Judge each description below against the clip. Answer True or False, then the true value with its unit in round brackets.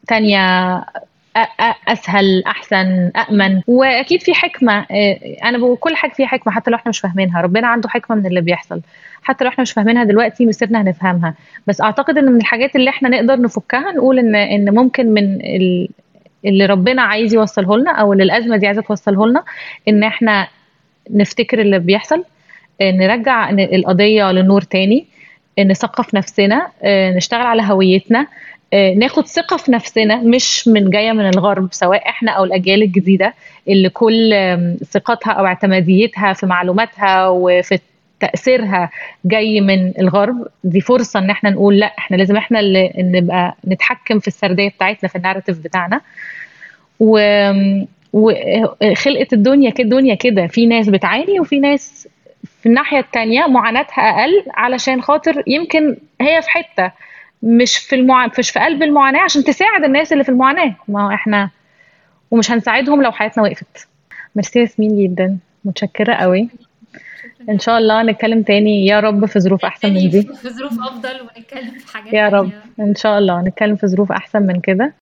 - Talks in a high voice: True (215 Hz)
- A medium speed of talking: False (150 wpm)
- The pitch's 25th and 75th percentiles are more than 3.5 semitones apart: True (4.0 semitones)